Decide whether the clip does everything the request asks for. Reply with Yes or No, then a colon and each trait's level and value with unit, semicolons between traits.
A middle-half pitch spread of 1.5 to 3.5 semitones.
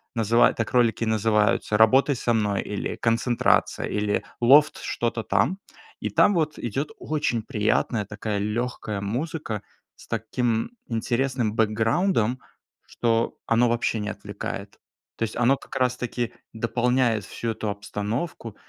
Yes: narrow, 2.6 semitones